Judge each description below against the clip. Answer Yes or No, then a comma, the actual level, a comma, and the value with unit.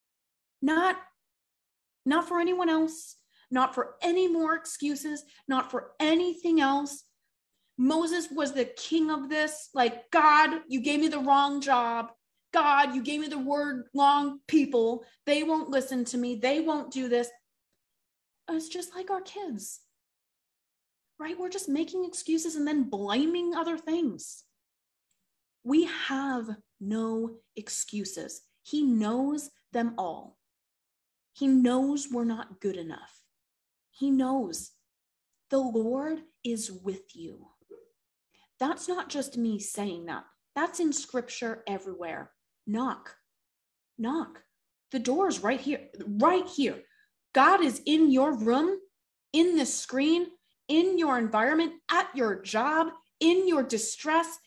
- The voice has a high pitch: Yes, very high, 285 Hz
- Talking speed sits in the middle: No, slow, 130 wpm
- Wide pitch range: No, average, 4.9 semitones